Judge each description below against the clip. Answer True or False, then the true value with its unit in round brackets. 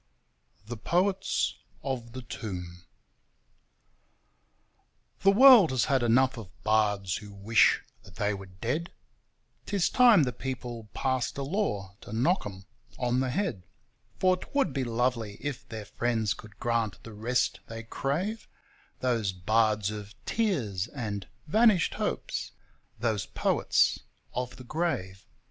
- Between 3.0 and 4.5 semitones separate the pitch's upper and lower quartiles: False (5.1 semitones)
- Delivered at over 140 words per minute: False (135 wpm)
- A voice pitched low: True (120 Hz)